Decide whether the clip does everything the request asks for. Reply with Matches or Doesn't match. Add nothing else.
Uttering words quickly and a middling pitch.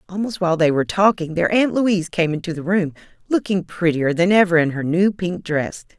Matches